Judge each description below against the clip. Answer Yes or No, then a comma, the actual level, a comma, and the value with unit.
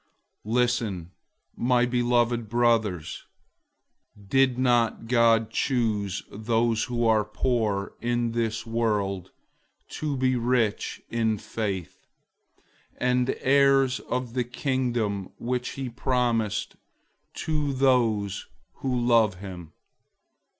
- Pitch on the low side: Yes, low, 120 Hz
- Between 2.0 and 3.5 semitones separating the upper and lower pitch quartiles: Yes, average, 2.7 semitones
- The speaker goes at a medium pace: No, slow, 95 wpm